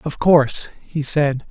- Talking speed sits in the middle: Yes, average, 160 wpm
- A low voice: No, medium, 145 Hz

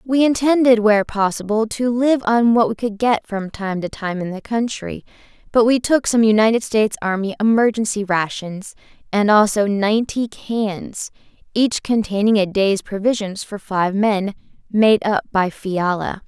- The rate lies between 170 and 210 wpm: No, average, 160 wpm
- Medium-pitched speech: No, high, 215 Hz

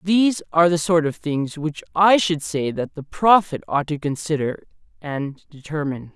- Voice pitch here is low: No, medium, 160 Hz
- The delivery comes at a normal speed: Yes, average, 175 wpm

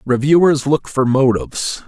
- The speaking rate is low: Yes, slow, 130 wpm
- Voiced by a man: Yes, male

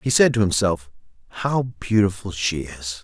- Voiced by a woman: No, male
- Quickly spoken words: No, average, 160 wpm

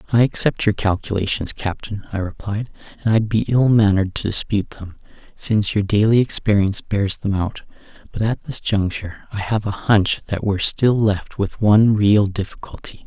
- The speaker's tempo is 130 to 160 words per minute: No, average, 175 wpm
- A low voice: Yes, low, 105 Hz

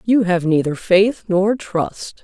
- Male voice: No, female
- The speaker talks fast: No, average, 160 wpm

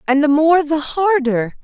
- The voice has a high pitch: Yes, very high, 295 Hz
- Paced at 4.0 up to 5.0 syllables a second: Yes, 4.1 syllables/s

